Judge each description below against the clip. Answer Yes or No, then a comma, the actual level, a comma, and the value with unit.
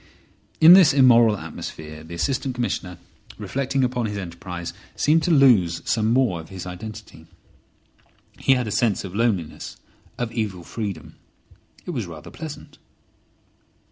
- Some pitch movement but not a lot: No, wide, 6.4 semitones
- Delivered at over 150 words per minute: No, average, 140 wpm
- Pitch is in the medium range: No, low, 110 Hz